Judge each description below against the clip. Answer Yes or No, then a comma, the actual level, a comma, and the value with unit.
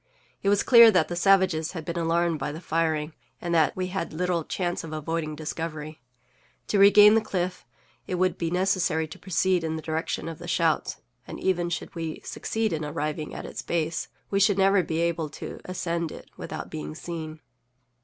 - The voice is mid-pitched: Yes, medium, 170 Hz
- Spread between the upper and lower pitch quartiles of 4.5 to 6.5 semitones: No, narrow, 2.6 semitones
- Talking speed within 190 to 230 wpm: Yes, average, 195 wpm